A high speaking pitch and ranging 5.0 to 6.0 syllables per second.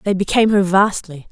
Yes: high, 195 Hz; 5.9 syllables/s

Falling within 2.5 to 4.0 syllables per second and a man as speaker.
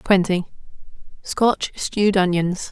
No: 3.6 syllables/s; female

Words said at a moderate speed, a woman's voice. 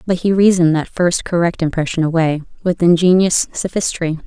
Yes: average, 155 wpm; female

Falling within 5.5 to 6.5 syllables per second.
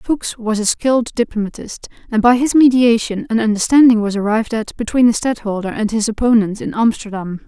Yes: 5.6 syllables/s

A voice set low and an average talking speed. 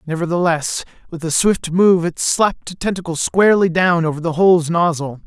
No: medium, 170 Hz; average, 170 wpm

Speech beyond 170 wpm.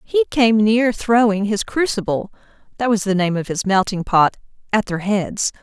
No: average, 160 wpm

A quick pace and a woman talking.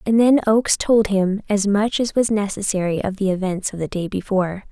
Yes: fast, 215 wpm; female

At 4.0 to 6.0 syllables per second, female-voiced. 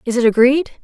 No: 6.6 syllables/s; female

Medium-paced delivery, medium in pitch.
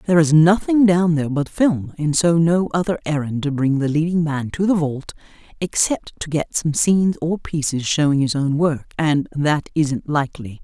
Yes: average, 195 wpm; medium, 155 Hz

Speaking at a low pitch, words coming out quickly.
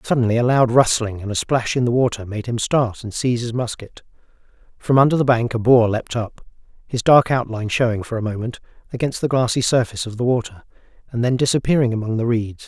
Yes: low, 120 Hz; fast, 210 wpm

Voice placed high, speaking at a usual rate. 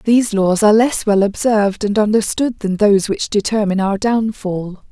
Yes: high, 210 Hz; average, 170 wpm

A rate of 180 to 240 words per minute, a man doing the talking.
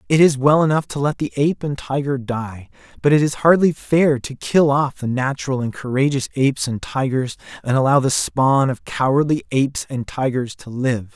Yes: average, 200 wpm; male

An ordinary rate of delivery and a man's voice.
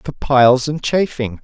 Yes: average, 165 wpm; male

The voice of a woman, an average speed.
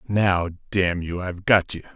No: male; average, 185 wpm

